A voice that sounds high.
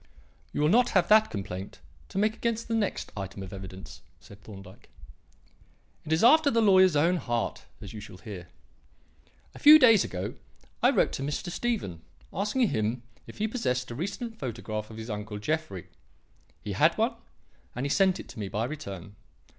No: low, 135 Hz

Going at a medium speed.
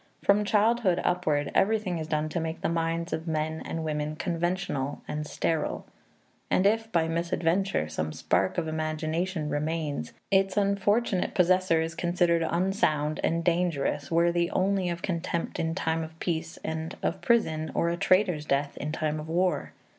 Yes: average, 160 wpm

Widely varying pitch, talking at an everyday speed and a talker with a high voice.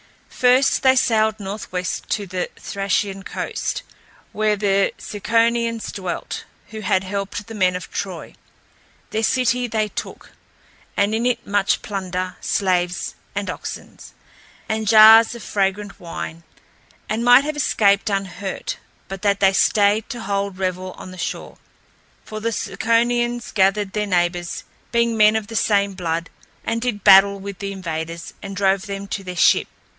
No: average, 2.7 semitones; average, 150 wpm; high, 200 Hz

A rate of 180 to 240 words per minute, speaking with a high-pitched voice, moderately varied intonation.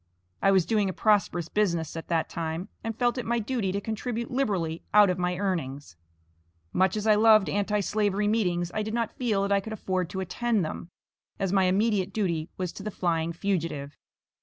Yes: average, 200 wpm; high, 195 Hz; average, 3.7 semitones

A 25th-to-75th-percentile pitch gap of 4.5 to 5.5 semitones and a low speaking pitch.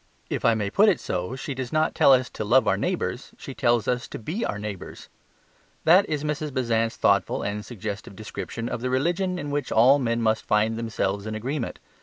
Yes: average, 4.9 semitones; low, 120 Hz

